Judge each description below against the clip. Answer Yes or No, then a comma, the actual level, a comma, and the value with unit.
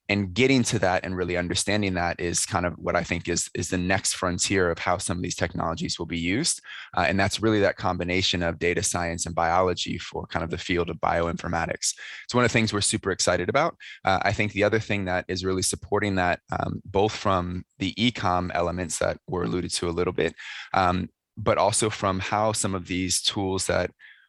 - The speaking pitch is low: Yes, very low, 90 Hz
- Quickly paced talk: Yes, fast, 220 wpm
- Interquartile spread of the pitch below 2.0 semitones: No, narrow, 2.4 semitones